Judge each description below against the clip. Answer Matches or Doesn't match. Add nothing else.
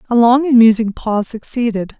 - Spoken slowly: Doesn't match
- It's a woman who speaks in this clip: Matches